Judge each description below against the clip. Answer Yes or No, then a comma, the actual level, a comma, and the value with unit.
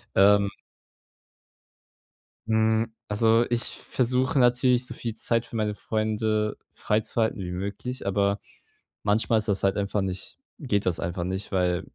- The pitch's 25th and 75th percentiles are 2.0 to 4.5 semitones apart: Yes, narrow, 2.6 semitones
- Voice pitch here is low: Yes, low, 105 Hz